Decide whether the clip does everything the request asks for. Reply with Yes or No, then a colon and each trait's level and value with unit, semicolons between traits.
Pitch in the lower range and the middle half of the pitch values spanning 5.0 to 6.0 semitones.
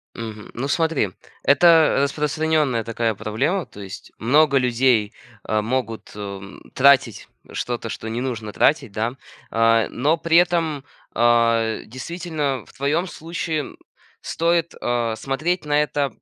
Yes: low, 130 Hz; wide, 5.5 semitones